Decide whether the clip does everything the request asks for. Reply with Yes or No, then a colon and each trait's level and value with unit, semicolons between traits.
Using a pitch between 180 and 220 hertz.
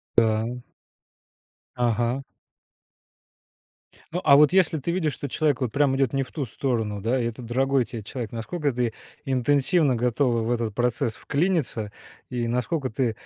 No: low, 125 Hz